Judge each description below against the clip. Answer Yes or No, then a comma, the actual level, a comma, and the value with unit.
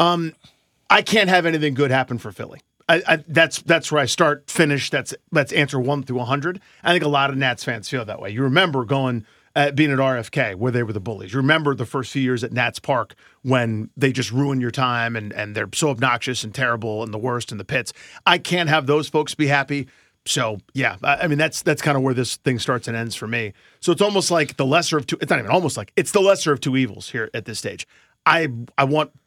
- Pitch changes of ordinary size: Yes, average, 4.1 semitones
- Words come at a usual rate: No, fast, 250 wpm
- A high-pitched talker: No, low, 135 Hz